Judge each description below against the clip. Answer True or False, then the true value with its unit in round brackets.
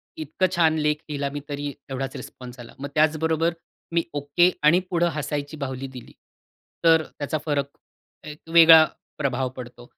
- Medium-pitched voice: True (150 Hz)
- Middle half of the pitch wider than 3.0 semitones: False (2.7 semitones)